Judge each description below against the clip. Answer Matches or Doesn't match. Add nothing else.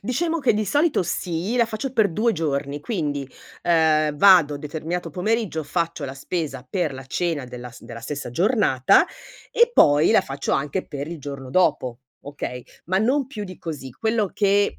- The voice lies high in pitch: Doesn't match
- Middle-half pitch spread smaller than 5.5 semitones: Doesn't match